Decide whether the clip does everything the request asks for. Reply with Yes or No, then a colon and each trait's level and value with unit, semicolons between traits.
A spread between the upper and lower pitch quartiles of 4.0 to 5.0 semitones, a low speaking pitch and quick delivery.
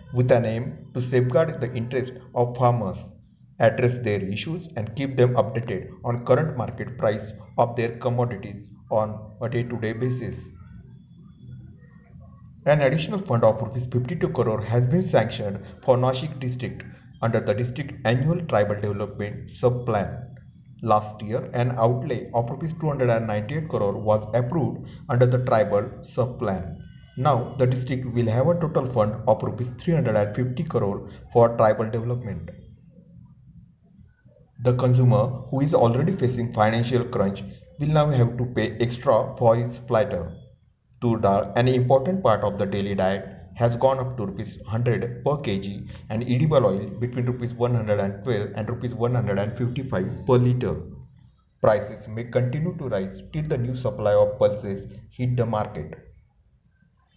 No: average, 3.2 semitones; low, 120 Hz; fast, 140 wpm